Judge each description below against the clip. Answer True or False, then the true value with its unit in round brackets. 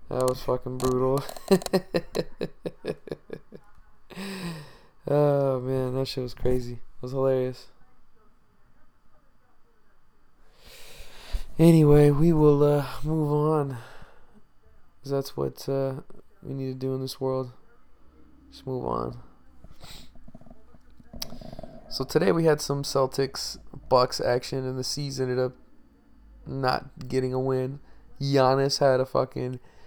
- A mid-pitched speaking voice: False (130 Hz)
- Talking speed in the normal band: False (105 wpm)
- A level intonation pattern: True (2.1 semitones)